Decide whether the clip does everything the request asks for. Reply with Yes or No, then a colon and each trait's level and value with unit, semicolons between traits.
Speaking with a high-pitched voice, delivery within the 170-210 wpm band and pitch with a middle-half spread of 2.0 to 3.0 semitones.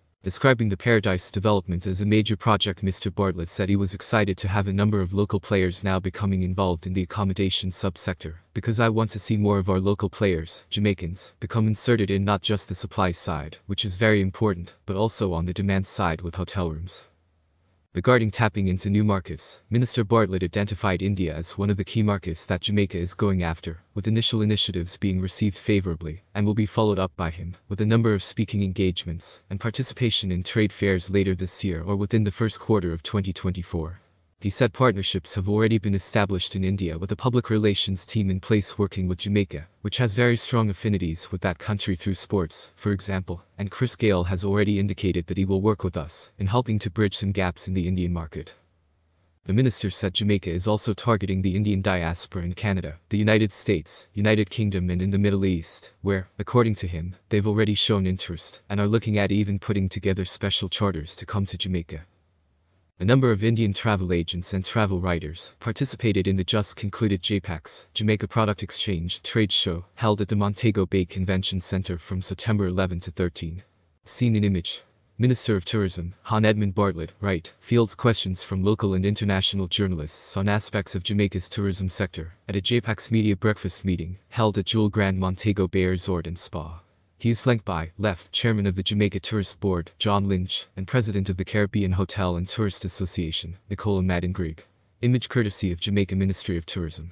No: low, 100 Hz; average, 190 wpm; narrow, 2.5 semitones